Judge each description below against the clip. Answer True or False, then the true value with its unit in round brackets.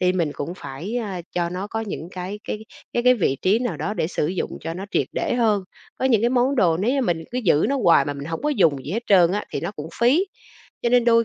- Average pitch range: False (5.8 semitones)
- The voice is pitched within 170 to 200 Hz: True (195 Hz)